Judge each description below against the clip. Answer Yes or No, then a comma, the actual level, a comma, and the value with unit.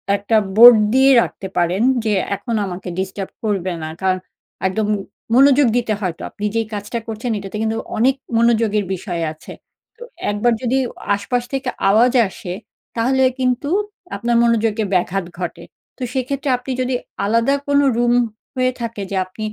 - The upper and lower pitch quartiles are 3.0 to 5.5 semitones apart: Yes, average, 3.9 semitones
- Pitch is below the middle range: No, high, 225 Hz